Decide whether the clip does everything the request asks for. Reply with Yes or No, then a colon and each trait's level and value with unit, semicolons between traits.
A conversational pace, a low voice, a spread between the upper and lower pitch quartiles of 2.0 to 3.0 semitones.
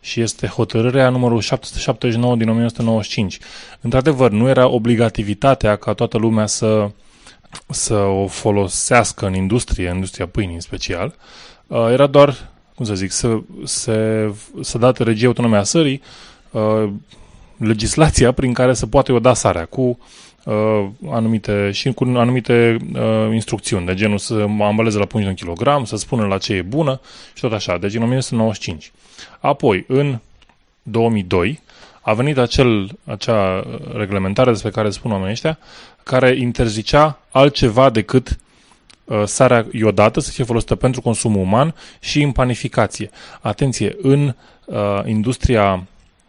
No: average, 135 wpm; low, 115 Hz; average, 3.5 semitones